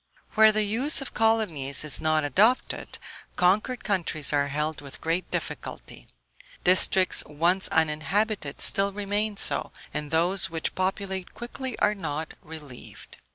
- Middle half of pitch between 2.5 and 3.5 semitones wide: No, average, 5.3 semitones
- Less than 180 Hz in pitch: No, medium, 185 Hz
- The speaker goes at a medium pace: No, slow, 130 wpm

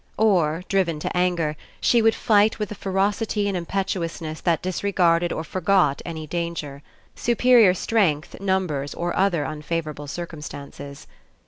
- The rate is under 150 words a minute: Yes, slow, 135 wpm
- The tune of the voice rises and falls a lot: No, average, 4.1 semitones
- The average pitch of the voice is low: No, medium, 175 Hz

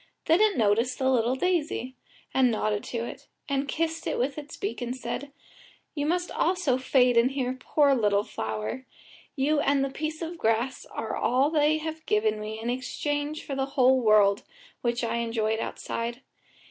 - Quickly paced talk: No, average, 175 wpm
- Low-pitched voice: No, very high, 260 Hz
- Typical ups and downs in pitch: Yes, average, 4.1 semitones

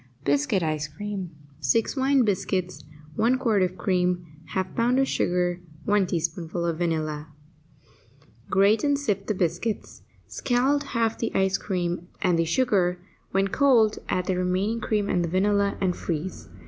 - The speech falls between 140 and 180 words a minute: Yes, average, 150 wpm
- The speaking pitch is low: No, high, 190 Hz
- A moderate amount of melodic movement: Yes, average, 3.9 semitones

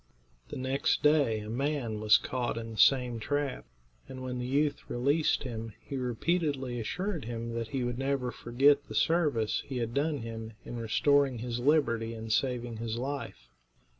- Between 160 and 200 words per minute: Yes, average, 170 wpm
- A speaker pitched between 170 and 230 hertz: No, low, 125 Hz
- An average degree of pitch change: Yes, average, 3.5 semitones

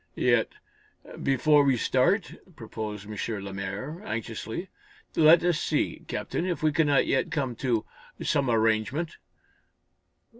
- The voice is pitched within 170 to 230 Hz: No, low, 130 Hz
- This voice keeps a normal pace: No, slow, 115 wpm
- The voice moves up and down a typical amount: No, wide, 5.8 semitones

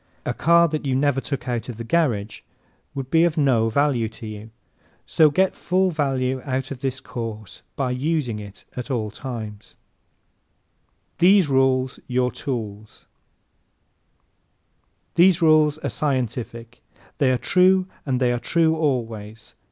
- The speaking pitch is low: Yes, low, 130 Hz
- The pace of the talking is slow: No, average, 145 wpm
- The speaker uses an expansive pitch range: No, average, 4.8 semitones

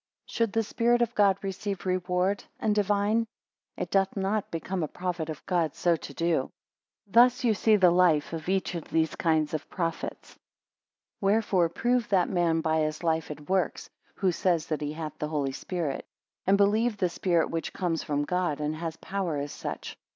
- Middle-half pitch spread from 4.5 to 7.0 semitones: No, average, 3.9 semitones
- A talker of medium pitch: Yes, medium, 180 Hz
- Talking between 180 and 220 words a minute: Yes, average, 190 wpm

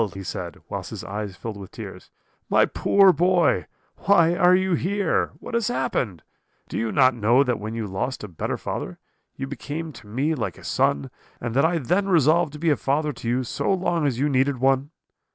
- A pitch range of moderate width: No, wide, 6.8 semitones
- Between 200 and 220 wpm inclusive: Yes, fast, 205 wpm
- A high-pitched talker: No, medium, 140 Hz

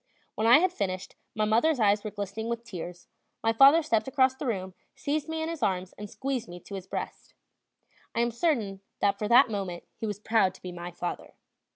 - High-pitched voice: Yes, high, 215 Hz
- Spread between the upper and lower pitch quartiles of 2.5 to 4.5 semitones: No, average, 5.2 semitones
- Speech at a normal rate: No, fast, 215 wpm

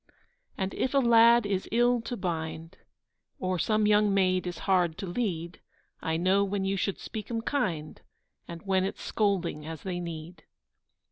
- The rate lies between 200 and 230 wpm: No, average, 165 wpm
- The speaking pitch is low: No, high, 190 Hz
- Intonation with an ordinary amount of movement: Yes, average, 3.7 semitones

